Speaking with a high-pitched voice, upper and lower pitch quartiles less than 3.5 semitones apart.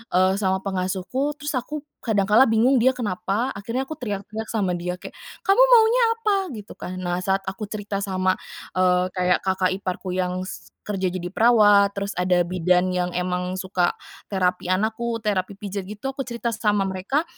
No: high, 200 Hz; average, 3.9 semitones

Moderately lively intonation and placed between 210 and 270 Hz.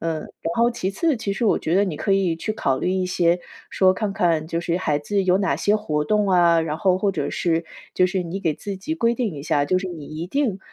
No: average, 3.4 semitones; medium, 185 Hz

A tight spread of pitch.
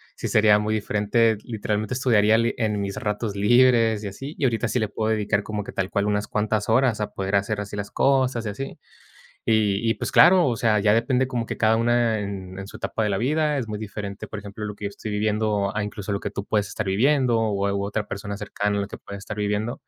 Yes: narrow, 2.0 semitones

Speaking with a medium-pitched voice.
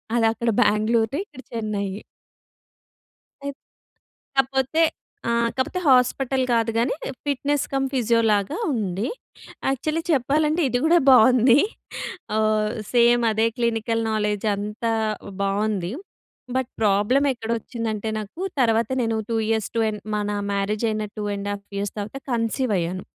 No: high, 225 Hz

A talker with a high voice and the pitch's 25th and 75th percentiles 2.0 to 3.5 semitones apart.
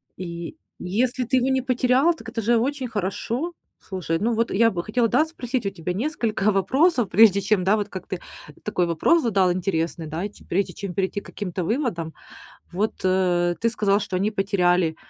No: high, 205 Hz; average, 4.7 semitones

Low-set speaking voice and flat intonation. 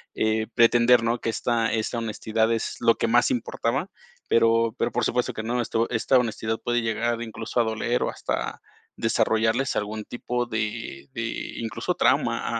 Yes: low, 115 Hz; narrow, 1.3 semitones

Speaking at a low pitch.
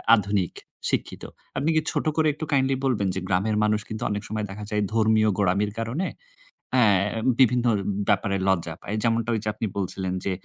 Yes: low, 105 Hz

